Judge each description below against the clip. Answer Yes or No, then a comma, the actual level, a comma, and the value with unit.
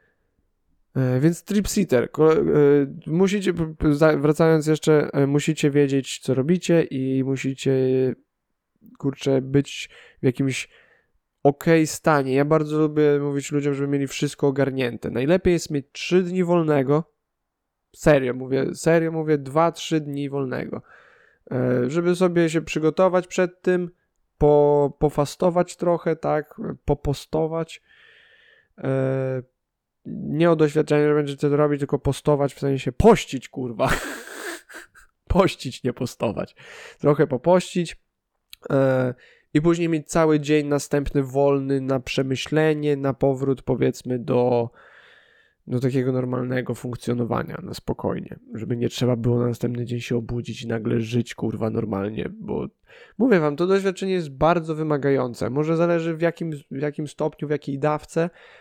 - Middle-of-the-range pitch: Yes, medium, 145 Hz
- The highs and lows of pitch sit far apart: No, average, 3.7 semitones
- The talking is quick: No, average, 125 wpm